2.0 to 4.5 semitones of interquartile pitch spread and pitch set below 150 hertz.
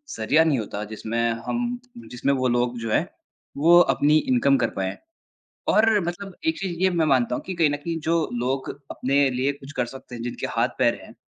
No: wide, 5.5 semitones; medium, 140 Hz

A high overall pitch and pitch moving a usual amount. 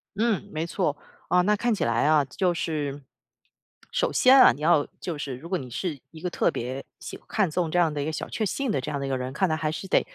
No: medium, 155 Hz; average, 4.4 semitones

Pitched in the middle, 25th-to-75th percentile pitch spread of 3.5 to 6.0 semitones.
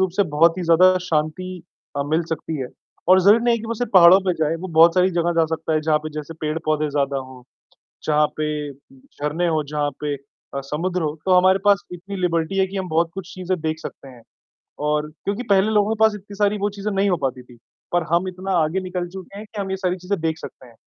Yes: medium, 175 Hz; average, 3.8 semitones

